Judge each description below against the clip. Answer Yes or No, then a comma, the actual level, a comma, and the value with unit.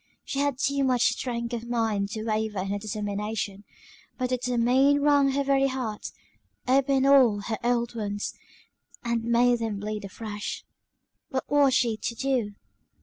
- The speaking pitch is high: Yes, high, 235 Hz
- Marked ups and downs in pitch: No, average, 3.7 semitones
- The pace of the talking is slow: No, average, 155 wpm